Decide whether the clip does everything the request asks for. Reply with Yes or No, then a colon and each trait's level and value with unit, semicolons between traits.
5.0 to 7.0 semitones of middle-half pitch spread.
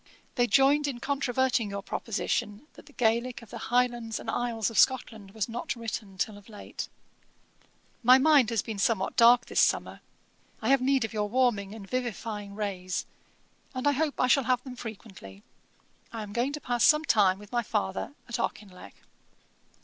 No: average, 3.5 semitones